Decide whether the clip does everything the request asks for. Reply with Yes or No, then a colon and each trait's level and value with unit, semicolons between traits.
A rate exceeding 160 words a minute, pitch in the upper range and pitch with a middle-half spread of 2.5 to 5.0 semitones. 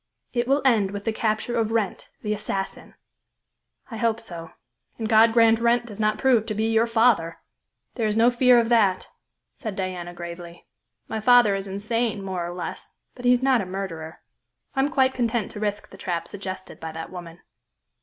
Yes: average, 195 wpm; high, 215 Hz; average, 3.8 semitones